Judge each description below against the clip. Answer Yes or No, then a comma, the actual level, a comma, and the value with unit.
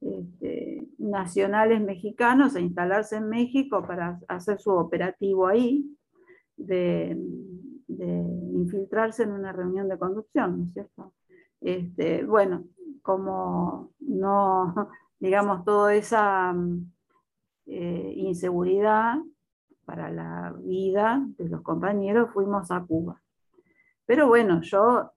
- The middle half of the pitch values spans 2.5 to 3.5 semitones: No, average, 4.2 semitones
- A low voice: No, high, 195 Hz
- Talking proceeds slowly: Yes, slow, 105 wpm